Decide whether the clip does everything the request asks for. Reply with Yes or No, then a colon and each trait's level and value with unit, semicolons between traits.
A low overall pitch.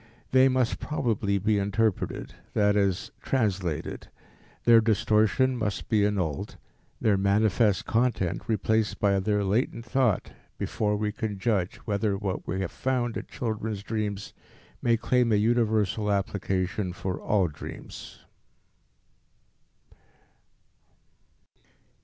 Yes: low, 105 Hz